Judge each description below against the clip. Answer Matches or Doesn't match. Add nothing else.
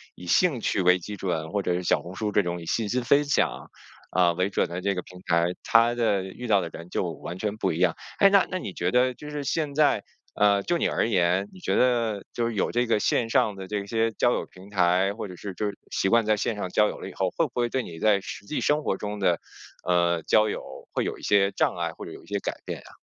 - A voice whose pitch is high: Doesn't match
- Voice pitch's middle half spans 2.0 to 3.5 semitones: Doesn't match